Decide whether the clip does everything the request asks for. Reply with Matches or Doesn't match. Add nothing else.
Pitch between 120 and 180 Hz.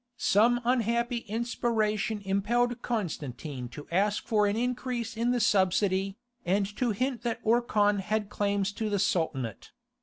Doesn't match